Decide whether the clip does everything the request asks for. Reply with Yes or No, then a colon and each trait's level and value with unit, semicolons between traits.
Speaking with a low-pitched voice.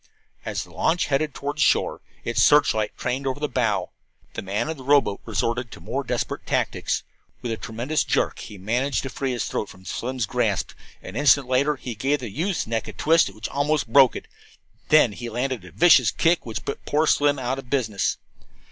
Yes: low, 130 Hz